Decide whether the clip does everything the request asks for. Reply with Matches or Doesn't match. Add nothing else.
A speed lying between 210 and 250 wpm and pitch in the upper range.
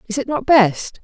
Matches